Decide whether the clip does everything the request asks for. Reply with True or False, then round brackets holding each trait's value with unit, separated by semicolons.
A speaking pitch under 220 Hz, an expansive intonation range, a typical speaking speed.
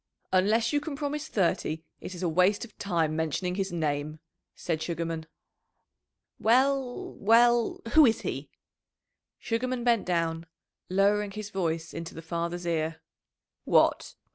False (185 Hz; 5.7 semitones; 130 wpm)